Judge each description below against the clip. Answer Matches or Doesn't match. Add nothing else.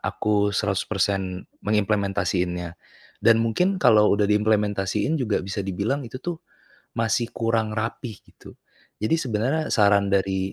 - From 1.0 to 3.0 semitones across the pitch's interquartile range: Matches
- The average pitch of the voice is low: Matches